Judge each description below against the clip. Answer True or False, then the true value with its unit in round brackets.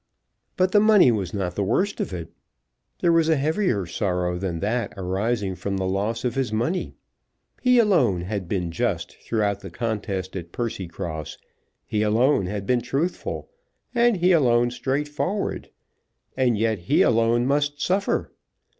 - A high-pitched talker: False (115 Hz)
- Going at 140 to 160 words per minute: True (155 wpm)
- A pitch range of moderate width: False (7.2 semitones)